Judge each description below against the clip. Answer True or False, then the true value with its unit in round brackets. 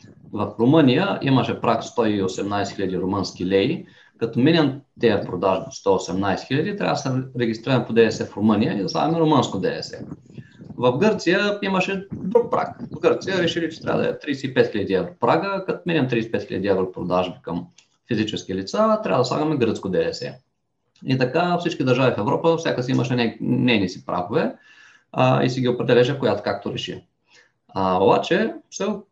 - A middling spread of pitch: False (6.5 semitones)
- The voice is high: False (125 Hz)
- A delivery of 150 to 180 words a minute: True (160 wpm)